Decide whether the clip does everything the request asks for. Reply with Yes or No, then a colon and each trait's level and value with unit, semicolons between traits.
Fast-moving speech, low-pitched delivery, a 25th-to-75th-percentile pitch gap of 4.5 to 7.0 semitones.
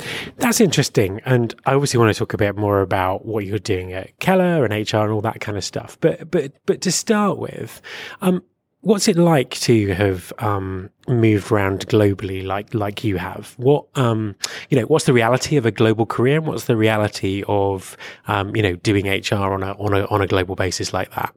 Yes: fast, 215 wpm; low, 110 Hz; average, 4.9 semitones